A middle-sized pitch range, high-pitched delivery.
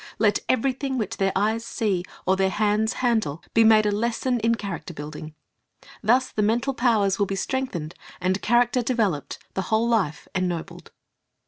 Yes: average, 3.8 semitones; high, 215 Hz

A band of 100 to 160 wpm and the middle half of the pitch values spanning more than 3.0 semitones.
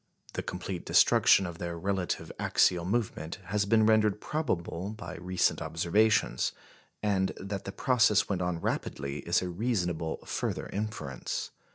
Yes: average, 140 wpm; average, 3.7 semitones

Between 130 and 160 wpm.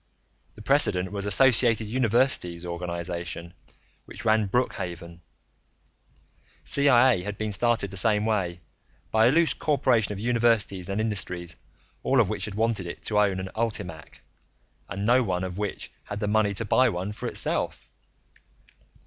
Yes: average, 150 wpm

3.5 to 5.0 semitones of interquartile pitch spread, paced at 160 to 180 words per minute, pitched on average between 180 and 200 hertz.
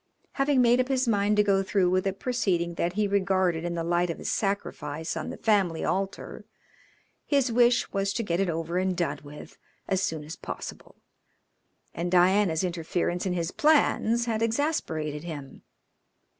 Yes: average, 4.2 semitones; average, 170 wpm; medium, 185 Hz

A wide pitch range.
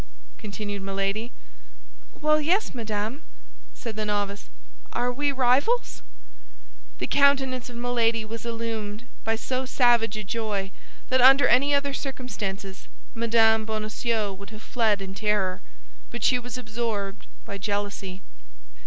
No: average, 3.5 semitones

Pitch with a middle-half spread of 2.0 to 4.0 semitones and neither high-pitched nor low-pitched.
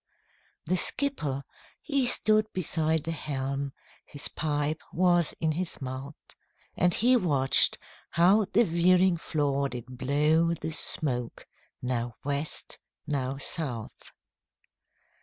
No: average, 4.4 semitones; medium, 155 Hz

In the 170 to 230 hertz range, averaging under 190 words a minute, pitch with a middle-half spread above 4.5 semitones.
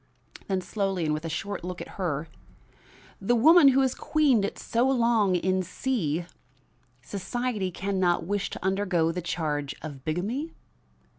Yes: high, 190 Hz; average, 155 wpm; wide, 5.5 semitones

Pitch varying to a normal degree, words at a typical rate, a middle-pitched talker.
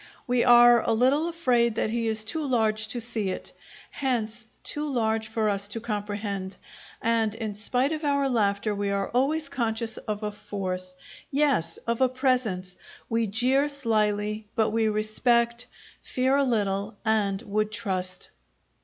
No: average, 3.1 semitones; average, 155 wpm; high, 225 Hz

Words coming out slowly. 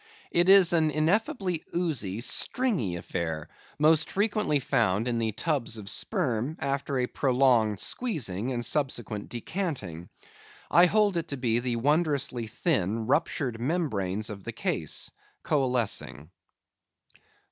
Yes: slow, 125 wpm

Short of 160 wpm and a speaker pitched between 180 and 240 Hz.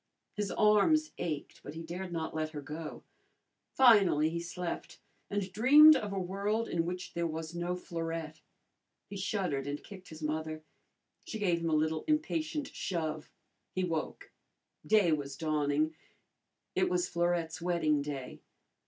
No: average, 150 wpm; medium, 170 Hz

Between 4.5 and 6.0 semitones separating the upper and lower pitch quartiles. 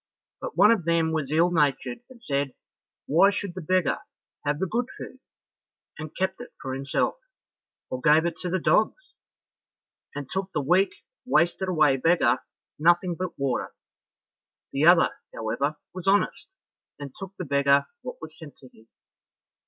Yes: average, 4.9 semitones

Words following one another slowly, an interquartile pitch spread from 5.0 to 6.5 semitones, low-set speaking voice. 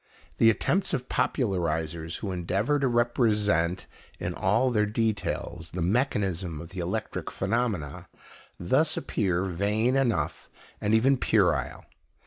Yes: slow, 120 wpm; average, 5.3 semitones; low, 105 Hz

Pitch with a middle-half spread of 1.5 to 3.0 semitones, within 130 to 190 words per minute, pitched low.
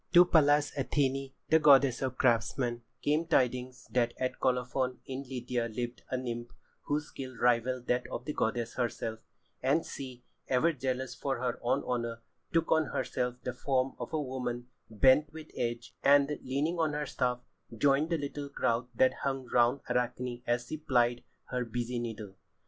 Yes: narrow, 2.5 semitones; average, 165 wpm; low, 130 Hz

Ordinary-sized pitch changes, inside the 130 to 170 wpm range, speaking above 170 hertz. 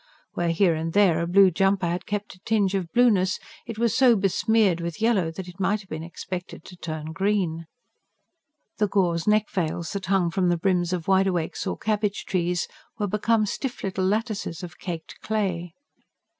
No: average, 3.2 semitones; average, 185 wpm; high, 190 Hz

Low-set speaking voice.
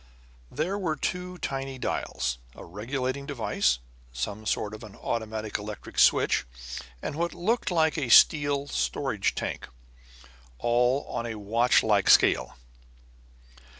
Yes: low, 125 Hz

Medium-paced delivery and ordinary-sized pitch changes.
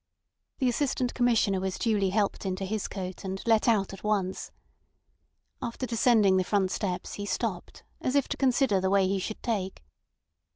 Yes: average, 170 wpm; average, 3.6 semitones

